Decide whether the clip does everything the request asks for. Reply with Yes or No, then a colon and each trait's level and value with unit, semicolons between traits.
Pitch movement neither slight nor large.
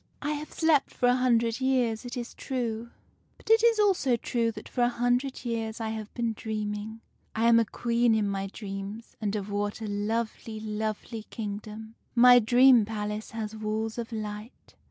No: narrow, 2.3 semitones